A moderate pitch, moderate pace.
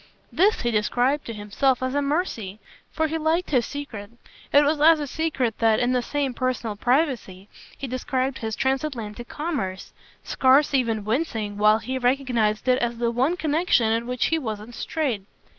No: very high, 255 Hz; average, 175 wpm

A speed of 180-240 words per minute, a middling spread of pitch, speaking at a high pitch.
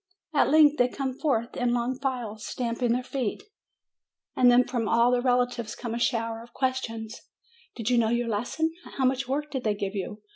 No: average, 195 wpm; narrow, 2.3 semitones; high, 245 Hz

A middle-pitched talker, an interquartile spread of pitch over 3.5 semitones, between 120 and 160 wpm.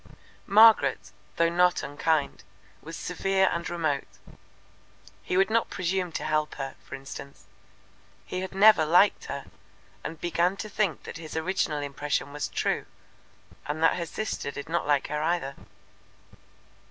Yes: medium, 165 Hz; average, 4.1 semitones; average, 145 wpm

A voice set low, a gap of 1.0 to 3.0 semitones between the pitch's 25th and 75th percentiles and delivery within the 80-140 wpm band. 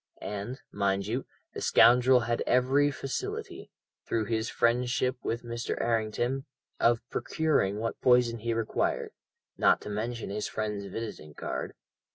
Yes: low, 115 Hz; narrow, 2.5 semitones; slow, 135 wpm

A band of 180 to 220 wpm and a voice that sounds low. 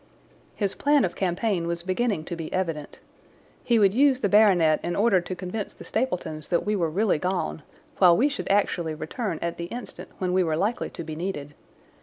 No: average, 200 wpm; medium, 185 Hz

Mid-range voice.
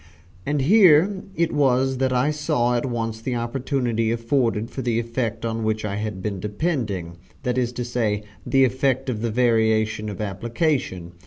No: low, 120 Hz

